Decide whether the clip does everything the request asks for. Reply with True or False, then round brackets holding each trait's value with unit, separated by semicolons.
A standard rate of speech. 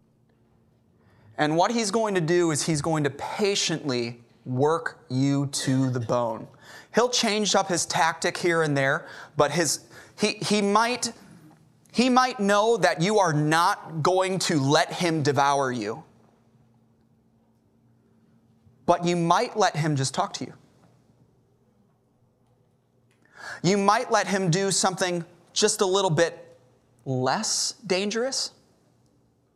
False (130 wpm)